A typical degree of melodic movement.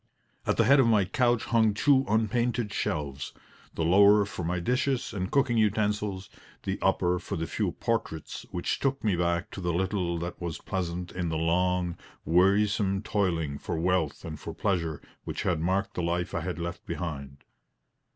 Yes: average, 3.7 semitones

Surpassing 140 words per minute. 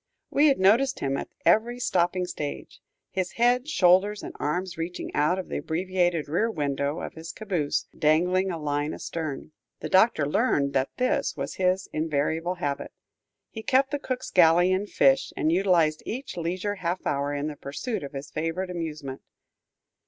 Yes: average, 165 wpm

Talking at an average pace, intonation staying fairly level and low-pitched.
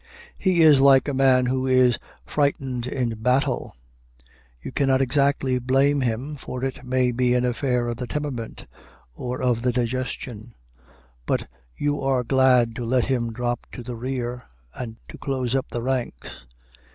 Yes: average, 160 wpm; narrow, 1.7 semitones; low, 125 Hz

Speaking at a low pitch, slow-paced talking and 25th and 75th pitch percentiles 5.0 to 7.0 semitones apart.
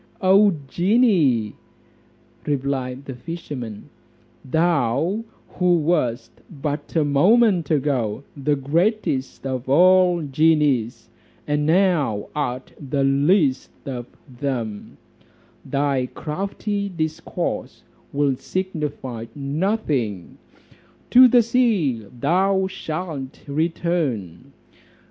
No: medium, 150 Hz; slow, 85 wpm; wide, 5.4 semitones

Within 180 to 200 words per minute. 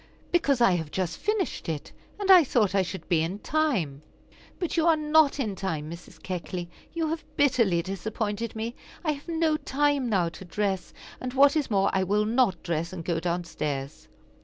Yes: average, 190 wpm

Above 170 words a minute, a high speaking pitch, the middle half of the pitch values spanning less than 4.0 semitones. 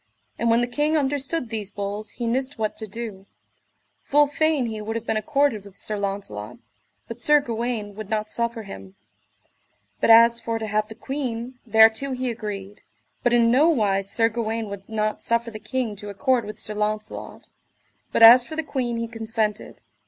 Yes: average, 180 wpm; high, 225 Hz; narrow, 2.6 semitones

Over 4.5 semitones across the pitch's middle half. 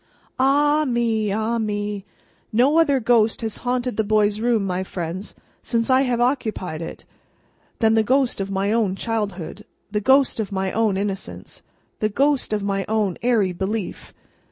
No: average, 3.5 semitones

